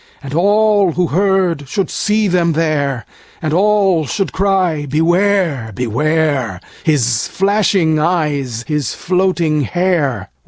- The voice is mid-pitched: Yes, medium, 165 Hz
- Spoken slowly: Yes, slow, 105 wpm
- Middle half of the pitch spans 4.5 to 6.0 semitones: Yes, average, 4.8 semitones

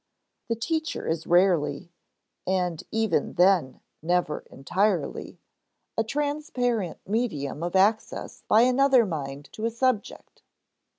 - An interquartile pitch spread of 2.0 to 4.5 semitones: No, wide, 5.5 semitones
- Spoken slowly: Yes, slow, 110 wpm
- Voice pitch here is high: Yes, high, 195 Hz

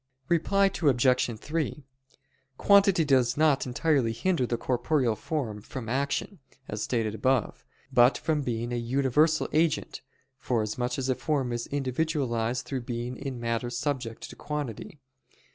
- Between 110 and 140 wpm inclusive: Yes, slow, 135 wpm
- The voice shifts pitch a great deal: No, average, 3.9 semitones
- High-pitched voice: No, low, 130 Hz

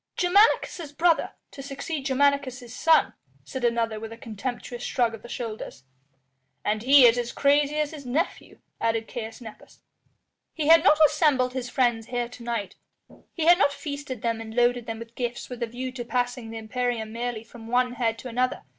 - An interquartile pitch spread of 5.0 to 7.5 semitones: No, average, 3.4 semitones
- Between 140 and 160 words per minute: No, average, 185 wpm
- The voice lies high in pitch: Yes, high, 245 Hz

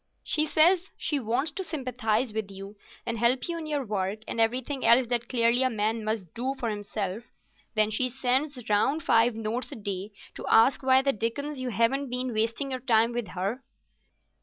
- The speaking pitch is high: Yes, high, 235 Hz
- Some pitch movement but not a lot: Yes, average, 3.5 semitones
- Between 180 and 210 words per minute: Yes, average, 190 wpm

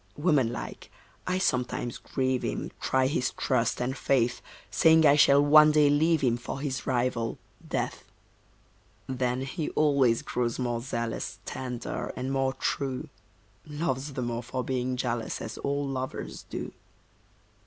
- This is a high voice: No, low, 130 Hz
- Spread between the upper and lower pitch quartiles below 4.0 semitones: Yes, average, 2.7 semitones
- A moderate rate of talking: Yes, average, 145 wpm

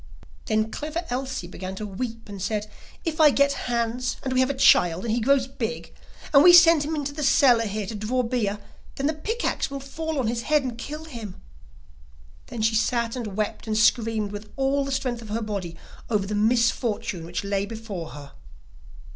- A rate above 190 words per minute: Yes, fast, 205 wpm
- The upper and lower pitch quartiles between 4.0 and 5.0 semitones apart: Yes, average, 4.4 semitones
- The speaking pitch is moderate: No, high, 235 Hz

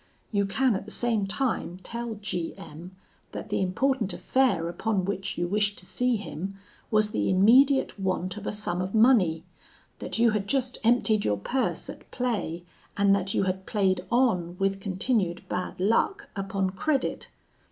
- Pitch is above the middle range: Yes, high, 200 Hz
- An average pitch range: Yes, average, 4.0 semitones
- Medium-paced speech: Yes, average, 170 wpm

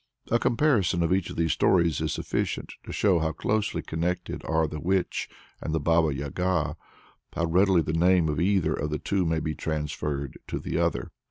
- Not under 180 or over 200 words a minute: Yes, average, 185 wpm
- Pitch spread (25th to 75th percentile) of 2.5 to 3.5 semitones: Yes, average, 3.1 semitones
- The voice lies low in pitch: Yes, very low, 85 Hz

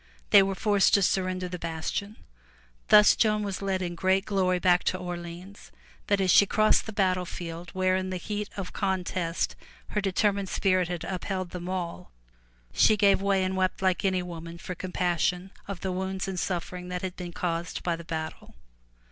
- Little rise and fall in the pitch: Yes, narrow, 1.6 semitones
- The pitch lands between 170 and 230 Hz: Yes, medium, 185 Hz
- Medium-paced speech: Yes, average, 180 wpm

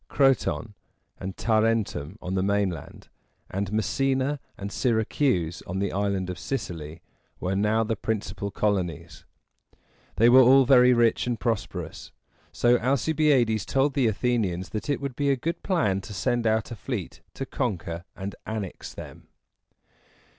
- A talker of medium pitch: No, low, 110 Hz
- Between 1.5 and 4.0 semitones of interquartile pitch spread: No, average, 4.7 semitones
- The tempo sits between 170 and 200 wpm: No, average, 150 wpm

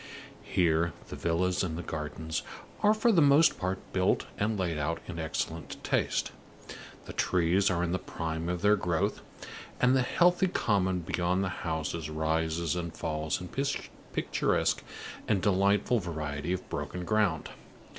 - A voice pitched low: Yes, very low, 90 Hz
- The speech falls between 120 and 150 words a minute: Yes, average, 145 wpm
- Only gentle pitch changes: No, average, 3.3 semitones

